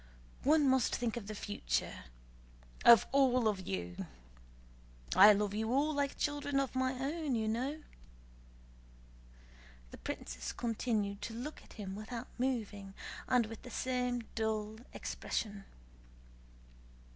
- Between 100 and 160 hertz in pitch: No, high, 230 Hz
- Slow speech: Yes, slow, 130 wpm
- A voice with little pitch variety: No, average, 4.0 semitones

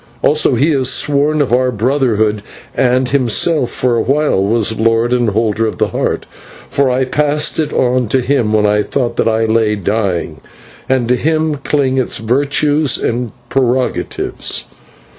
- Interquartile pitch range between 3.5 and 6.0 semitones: Yes, average, 3.9 semitones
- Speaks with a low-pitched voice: Yes, low, 125 Hz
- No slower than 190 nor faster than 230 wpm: No, average, 160 wpm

